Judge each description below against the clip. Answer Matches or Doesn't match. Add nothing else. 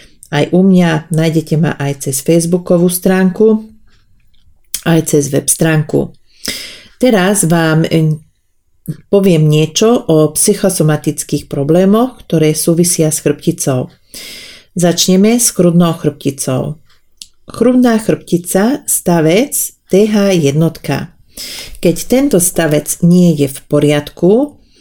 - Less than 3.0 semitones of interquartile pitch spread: Doesn't match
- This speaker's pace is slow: Matches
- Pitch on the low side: Doesn't match